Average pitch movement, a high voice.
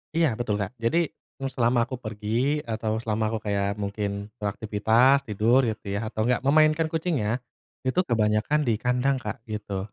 No: average, 3.9 semitones; low, 115 Hz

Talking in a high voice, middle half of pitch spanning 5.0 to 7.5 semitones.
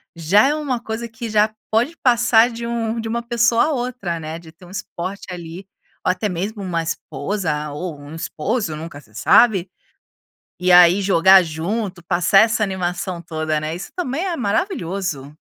Yes: high, 195 Hz; wide, 5.4 semitones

